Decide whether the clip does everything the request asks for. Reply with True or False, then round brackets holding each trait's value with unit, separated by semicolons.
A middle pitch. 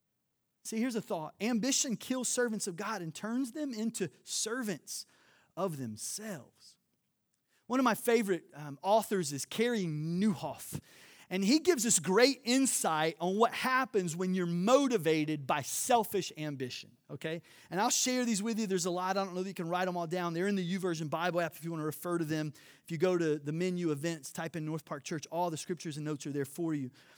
True (180 Hz)